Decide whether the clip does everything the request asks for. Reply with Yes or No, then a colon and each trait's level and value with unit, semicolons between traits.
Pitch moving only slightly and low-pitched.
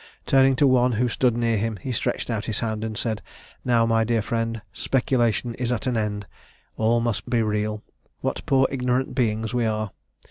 Yes: narrow, 2.2 semitones; low, 115 Hz